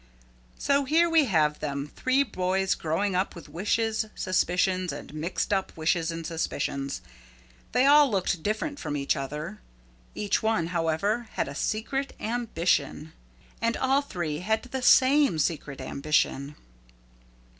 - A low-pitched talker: No, medium, 185 Hz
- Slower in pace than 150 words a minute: Yes, slow, 135 wpm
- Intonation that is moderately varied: No, wide, 6.7 semitones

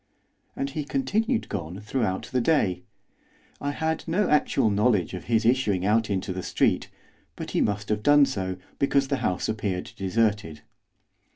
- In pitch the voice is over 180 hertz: No, low, 110 Hz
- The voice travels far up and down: Yes, wide, 6.5 semitones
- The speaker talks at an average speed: Yes, average, 160 wpm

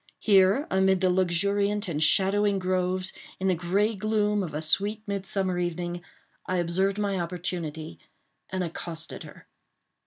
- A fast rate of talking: No, slow, 135 wpm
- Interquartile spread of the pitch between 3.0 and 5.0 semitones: No, narrow, 2.4 semitones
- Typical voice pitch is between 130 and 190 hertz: Yes, medium, 185 Hz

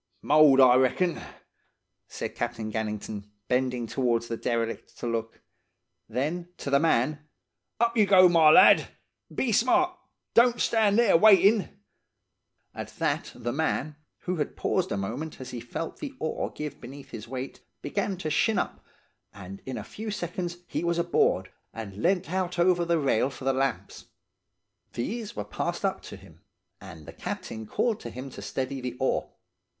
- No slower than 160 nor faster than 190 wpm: Yes, average, 165 wpm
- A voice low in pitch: No, medium, 145 Hz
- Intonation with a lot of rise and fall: Yes, wide, 7.3 semitones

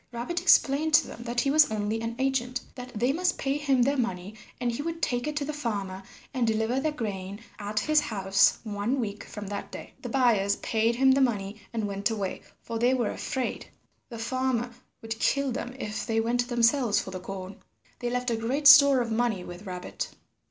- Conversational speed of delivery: No, fast, 210 wpm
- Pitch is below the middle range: No, high, 235 Hz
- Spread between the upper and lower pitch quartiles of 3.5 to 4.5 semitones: Yes, average, 4.2 semitones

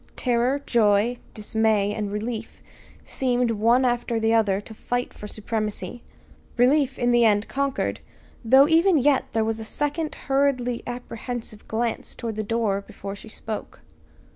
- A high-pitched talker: Yes, high, 230 Hz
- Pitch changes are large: No, narrow, 2.5 semitones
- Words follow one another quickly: No, average, 145 wpm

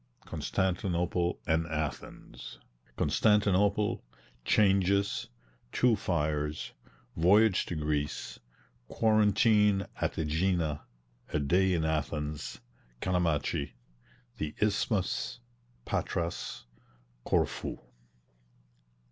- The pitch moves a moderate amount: Yes, average, 4.8 semitones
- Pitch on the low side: Yes, very low, 90 Hz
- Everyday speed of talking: No, slow, 70 wpm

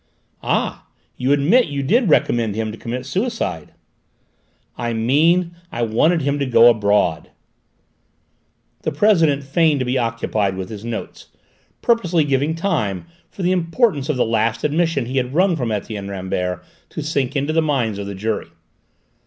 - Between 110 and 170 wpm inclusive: Yes, average, 160 wpm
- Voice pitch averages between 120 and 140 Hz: Yes, low, 135 Hz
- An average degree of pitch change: No, wide, 6.5 semitones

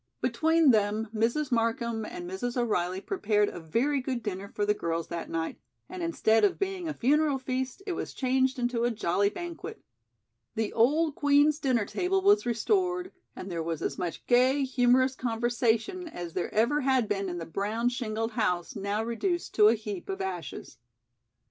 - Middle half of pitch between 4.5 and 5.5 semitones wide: Yes, average, 5.2 semitones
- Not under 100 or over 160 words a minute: No, average, 175 wpm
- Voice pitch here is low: No, high, 235 Hz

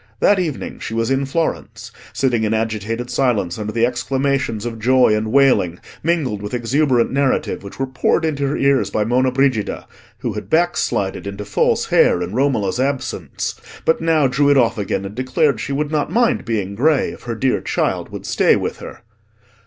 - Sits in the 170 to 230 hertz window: No, low, 125 Hz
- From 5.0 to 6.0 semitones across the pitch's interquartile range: No, average, 4.4 semitones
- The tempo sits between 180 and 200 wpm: Yes, average, 185 wpm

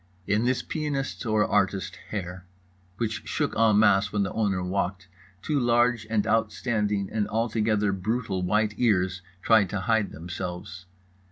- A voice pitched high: No, low, 105 Hz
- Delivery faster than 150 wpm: No, average, 145 wpm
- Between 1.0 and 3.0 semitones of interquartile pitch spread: Yes, average, 2.7 semitones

